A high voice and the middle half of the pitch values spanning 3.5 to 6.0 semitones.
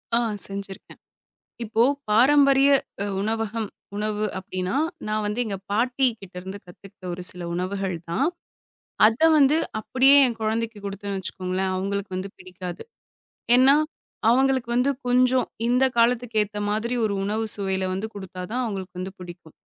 Yes: high, 210 Hz; average, 4.3 semitones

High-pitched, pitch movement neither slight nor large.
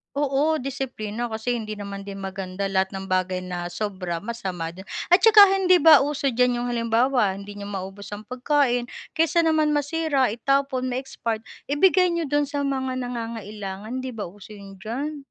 No: high, 240 Hz; wide, 5.9 semitones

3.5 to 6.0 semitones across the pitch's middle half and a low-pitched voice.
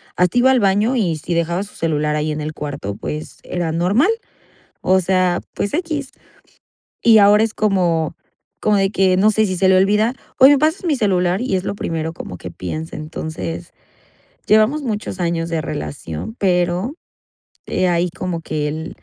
No: average, 4.6 semitones; medium, 185 Hz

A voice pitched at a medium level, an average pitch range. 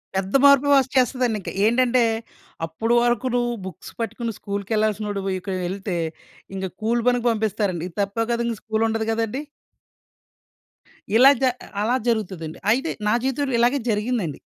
No: high, 225 Hz; average, 3.4 semitones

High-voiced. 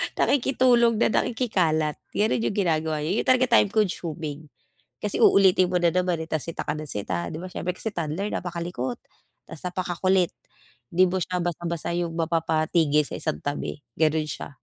No: medium, 175 Hz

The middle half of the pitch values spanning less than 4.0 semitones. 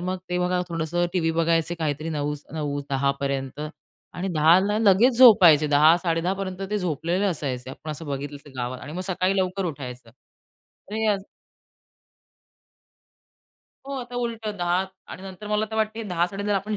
No: average, 4.7 semitones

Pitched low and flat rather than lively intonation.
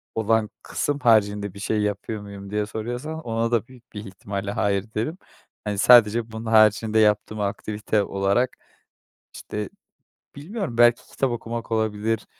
Yes: low, 110 Hz; narrow, 2.2 semitones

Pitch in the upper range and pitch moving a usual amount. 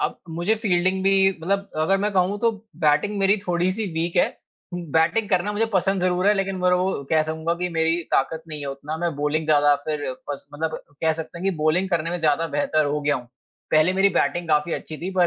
No: medium, 170 Hz; average, 3.5 semitones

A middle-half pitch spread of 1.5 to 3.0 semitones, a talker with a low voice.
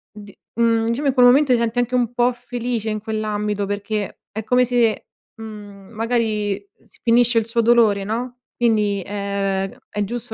No: average, 2.7 semitones; high, 225 Hz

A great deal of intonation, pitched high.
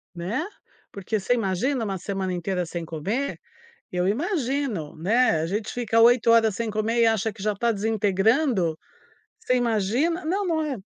No: average, 4.4 semitones; high, 220 Hz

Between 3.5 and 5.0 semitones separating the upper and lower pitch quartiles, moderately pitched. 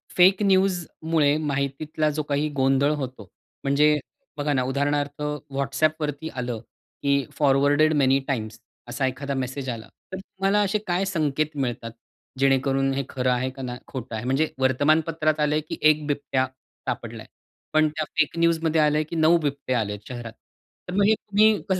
No: average, 2.9 semitones; medium, 145 Hz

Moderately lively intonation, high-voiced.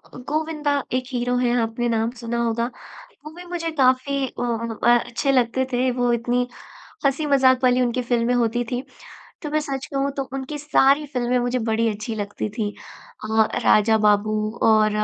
Yes: average, 3.0 semitones; high, 245 Hz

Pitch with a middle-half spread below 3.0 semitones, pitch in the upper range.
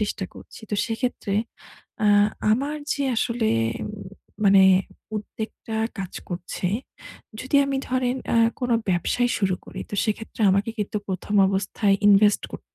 No: average, 3.8 semitones; high, 210 Hz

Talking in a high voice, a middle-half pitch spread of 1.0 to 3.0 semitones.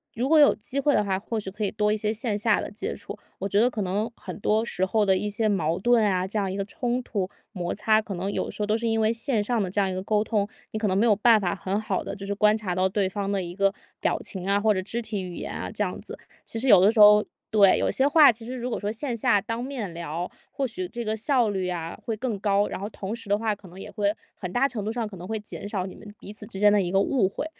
Yes: high, 210 Hz; narrow, 2.5 semitones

